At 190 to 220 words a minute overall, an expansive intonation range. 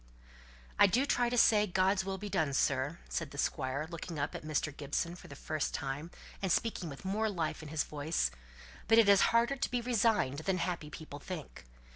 Yes: average, 200 wpm; wide, 5.9 semitones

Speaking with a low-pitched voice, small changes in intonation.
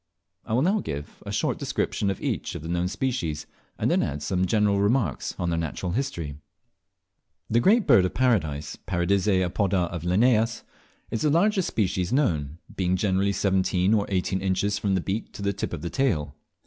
No: very low, 95 Hz; average, 4.3 semitones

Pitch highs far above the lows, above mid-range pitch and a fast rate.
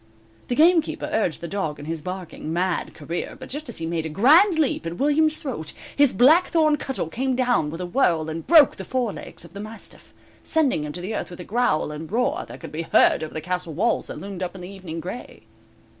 Yes: wide, 8.4 semitones; high, 195 Hz; fast, 225 wpm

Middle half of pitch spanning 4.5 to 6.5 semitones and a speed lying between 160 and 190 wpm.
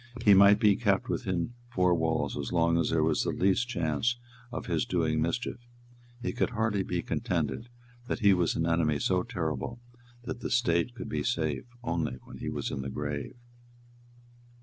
Yes: average, 5.3 semitones; average, 180 wpm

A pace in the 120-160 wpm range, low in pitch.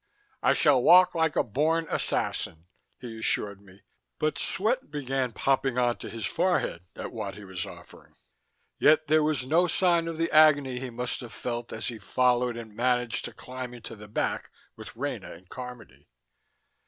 No: average, 170 wpm; low, 125 Hz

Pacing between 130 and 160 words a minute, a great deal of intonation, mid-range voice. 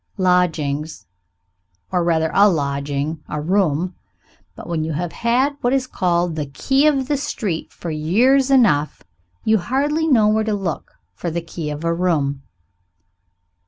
Yes: average, 155 wpm; wide, 7.1 semitones; medium, 175 Hz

